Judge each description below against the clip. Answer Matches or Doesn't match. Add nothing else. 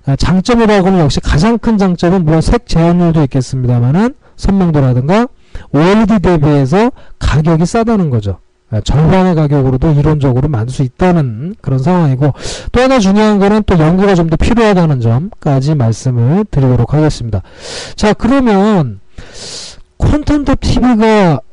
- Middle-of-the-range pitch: Matches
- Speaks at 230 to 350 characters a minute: Matches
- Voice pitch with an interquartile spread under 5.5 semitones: Doesn't match